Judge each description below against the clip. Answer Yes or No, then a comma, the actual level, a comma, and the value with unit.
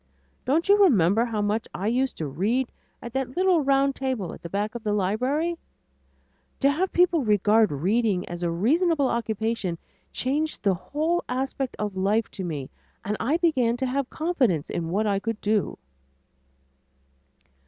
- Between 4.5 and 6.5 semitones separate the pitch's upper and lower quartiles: Yes, wide, 5.6 semitones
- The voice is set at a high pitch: Yes, high, 230 Hz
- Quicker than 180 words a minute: No, average, 165 wpm